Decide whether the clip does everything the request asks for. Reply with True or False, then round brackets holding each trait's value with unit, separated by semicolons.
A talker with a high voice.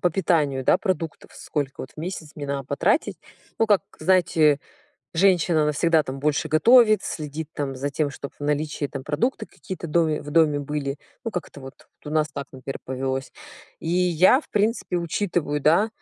False (155 Hz)